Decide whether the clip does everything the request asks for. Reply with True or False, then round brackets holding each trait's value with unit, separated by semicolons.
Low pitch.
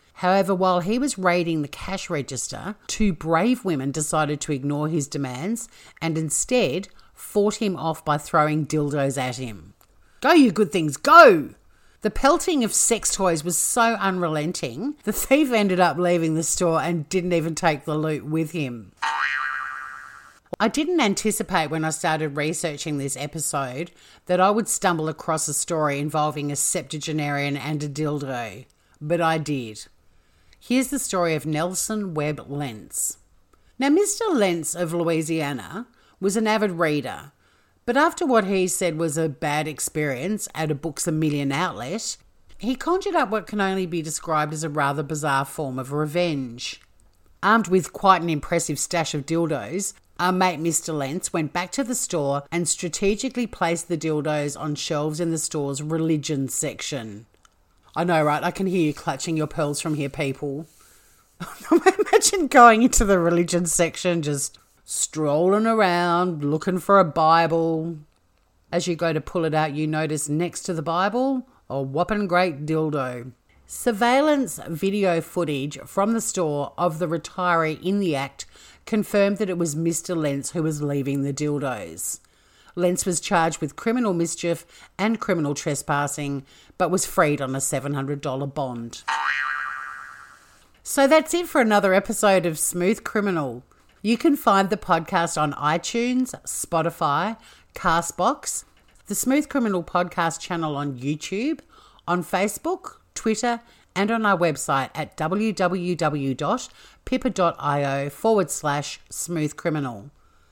False (165 Hz)